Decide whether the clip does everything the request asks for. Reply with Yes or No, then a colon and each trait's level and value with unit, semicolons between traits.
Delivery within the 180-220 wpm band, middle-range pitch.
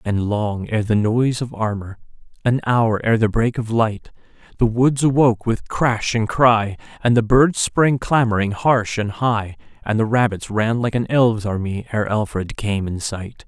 No: average, 185 wpm; low, 110 Hz